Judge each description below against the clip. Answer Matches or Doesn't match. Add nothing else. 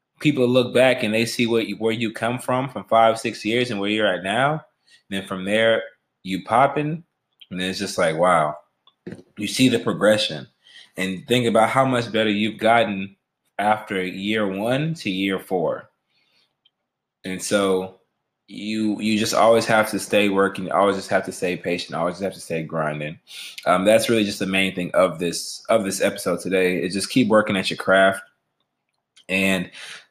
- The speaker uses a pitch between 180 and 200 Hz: Doesn't match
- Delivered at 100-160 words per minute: Doesn't match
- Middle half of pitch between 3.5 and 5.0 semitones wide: Doesn't match